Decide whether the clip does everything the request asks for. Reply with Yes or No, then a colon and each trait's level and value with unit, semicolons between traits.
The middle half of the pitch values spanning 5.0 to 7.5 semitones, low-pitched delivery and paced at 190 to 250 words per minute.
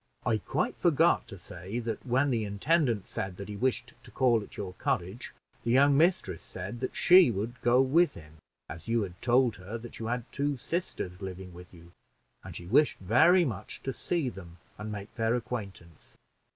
Yes: wide, 5.4 semitones; low, 115 Hz; average, 195 wpm